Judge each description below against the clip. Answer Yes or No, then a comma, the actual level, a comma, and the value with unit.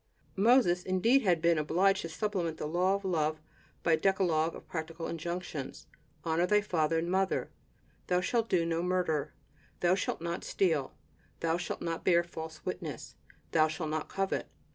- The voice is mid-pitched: Yes, medium, 170 Hz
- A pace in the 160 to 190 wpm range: Yes, average, 165 wpm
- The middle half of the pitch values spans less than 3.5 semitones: Yes, narrow, 2.6 semitones